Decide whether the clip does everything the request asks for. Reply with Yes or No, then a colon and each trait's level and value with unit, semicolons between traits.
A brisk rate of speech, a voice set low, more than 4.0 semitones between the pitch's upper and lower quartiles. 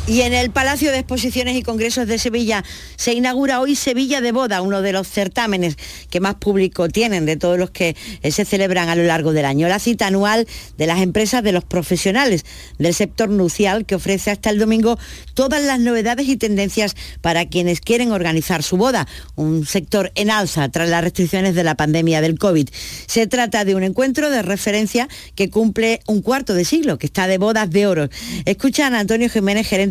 No: fast, 195 wpm; high, 205 Hz; average, 4.7 semitones